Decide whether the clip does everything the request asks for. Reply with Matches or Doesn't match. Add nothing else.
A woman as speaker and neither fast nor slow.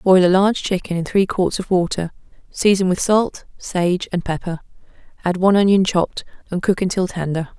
Matches